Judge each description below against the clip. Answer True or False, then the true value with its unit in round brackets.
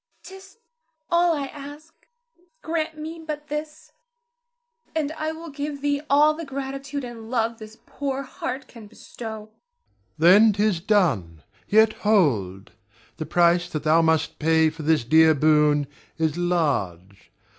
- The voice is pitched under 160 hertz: False (220 Hz)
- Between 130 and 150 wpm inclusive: True (145 wpm)